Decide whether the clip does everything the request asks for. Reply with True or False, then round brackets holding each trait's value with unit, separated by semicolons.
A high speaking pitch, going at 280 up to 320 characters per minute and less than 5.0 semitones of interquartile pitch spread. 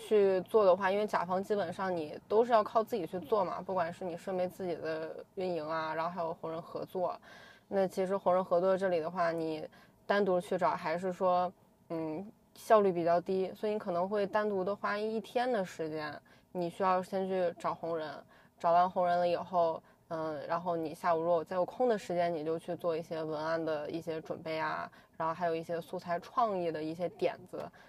False (175 Hz; 300 characters per minute; 2.6 semitones)